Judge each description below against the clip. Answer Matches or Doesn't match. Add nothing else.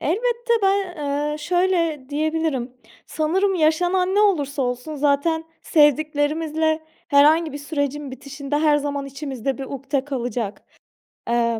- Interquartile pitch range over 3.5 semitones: Doesn't match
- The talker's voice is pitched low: Doesn't match